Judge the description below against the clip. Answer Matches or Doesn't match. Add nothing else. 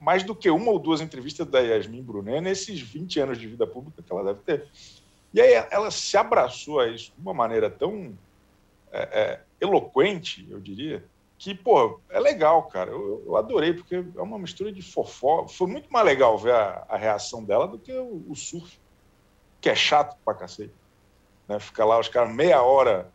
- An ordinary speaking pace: Doesn't match